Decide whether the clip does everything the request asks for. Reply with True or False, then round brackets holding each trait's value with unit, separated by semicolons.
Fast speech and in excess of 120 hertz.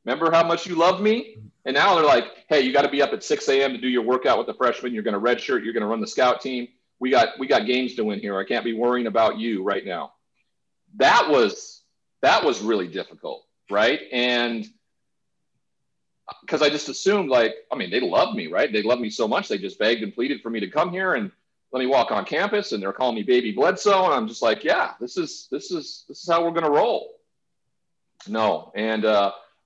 True (240 wpm; 140 Hz)